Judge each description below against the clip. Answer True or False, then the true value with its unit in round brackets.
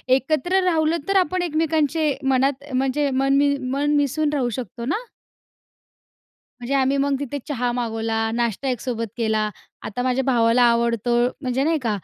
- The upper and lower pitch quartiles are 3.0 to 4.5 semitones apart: True (3.6 semitones)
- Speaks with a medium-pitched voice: False (265 Hz)